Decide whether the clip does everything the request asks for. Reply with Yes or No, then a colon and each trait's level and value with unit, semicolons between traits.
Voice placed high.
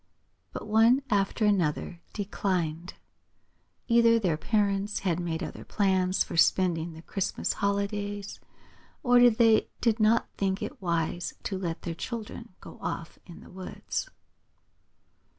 Yes: high, 195 Hz